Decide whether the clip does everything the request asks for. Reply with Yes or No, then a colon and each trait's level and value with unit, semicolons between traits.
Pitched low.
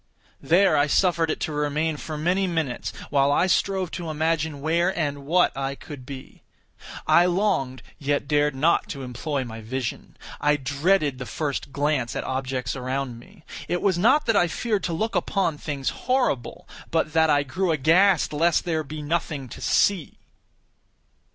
No: medium, 155 Hz